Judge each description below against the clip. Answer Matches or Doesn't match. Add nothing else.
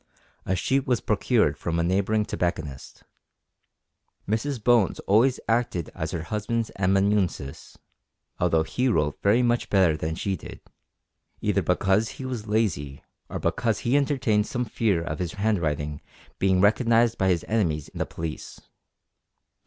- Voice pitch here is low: Matches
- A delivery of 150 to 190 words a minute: Doesn't match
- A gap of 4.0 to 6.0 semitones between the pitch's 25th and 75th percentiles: Matches